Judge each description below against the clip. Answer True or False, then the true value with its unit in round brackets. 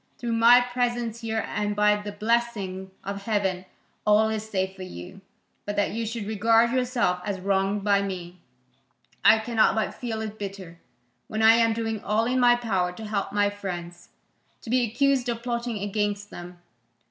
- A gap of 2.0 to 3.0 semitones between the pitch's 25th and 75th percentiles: True (2.7 semitones)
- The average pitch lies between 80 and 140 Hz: False (210 Hz)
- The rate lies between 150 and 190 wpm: True (175 wpm)